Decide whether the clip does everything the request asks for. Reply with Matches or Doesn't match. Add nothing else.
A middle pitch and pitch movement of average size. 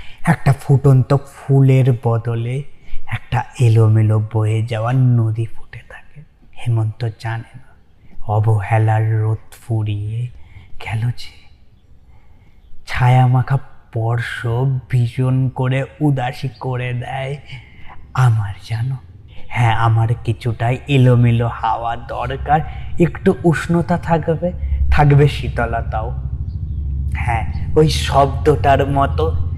Doesn't match